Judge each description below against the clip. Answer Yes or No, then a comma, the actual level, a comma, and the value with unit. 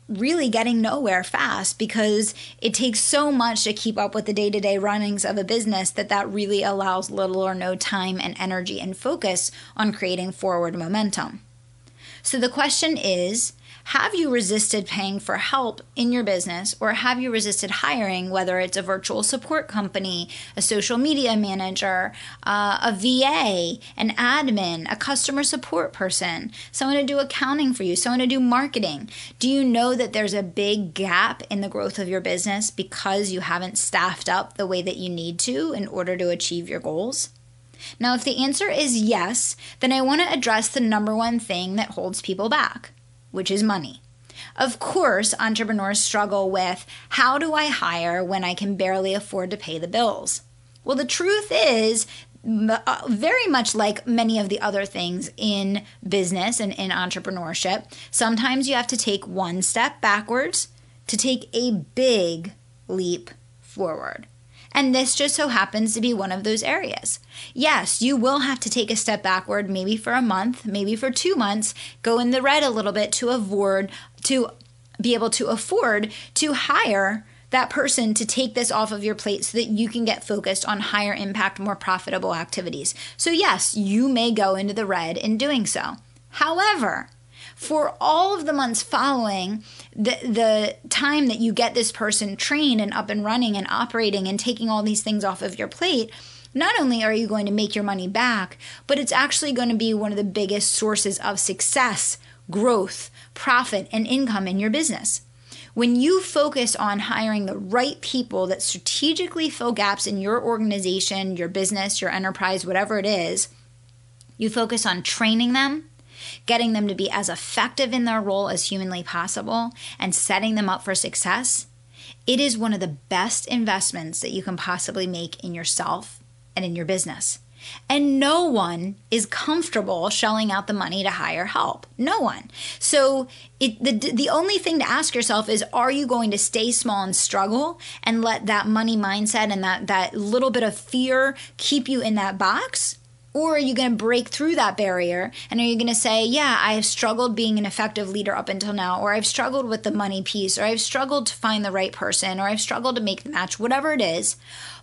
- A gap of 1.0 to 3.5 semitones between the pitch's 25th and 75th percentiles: No, average, 4.4 semitones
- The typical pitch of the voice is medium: No, high, 210 Hz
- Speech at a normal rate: Yes, average, 185 wpm